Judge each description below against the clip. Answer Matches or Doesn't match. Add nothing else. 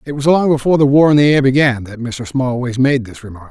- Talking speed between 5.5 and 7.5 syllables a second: Matches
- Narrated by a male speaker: Matches